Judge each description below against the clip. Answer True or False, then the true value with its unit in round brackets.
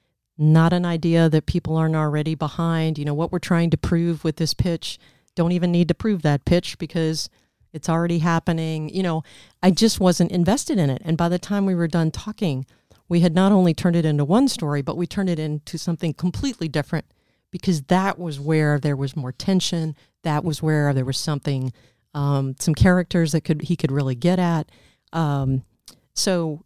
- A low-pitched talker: False (165 Hz)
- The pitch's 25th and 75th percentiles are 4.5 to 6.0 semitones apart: False (2.6 semitones)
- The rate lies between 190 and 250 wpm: True (200 wpm)